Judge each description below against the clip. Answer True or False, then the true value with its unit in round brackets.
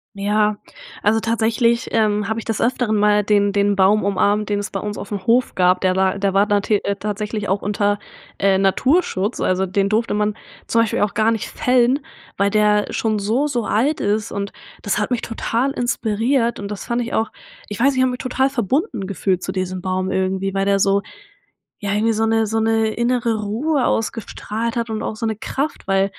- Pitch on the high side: True (210 Hz)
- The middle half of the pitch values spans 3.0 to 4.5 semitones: False (2.5 semitones)